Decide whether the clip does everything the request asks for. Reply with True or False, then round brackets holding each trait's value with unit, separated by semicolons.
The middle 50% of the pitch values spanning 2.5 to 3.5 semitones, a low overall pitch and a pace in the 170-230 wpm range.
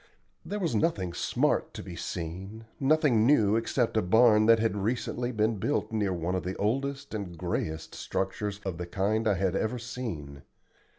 False (4.2 semitones; 110 Hz; 175 wpm)